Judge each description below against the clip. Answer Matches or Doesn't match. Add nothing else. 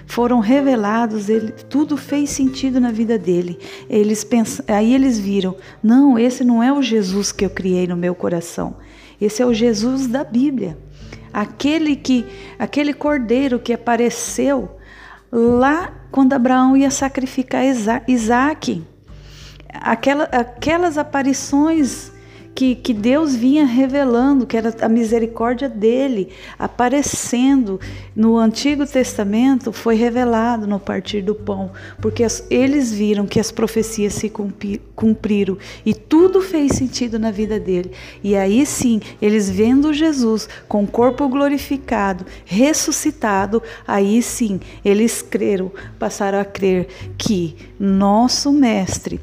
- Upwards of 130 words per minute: Doesn't match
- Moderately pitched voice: Doesn't match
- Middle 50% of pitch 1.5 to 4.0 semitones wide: Doesn't match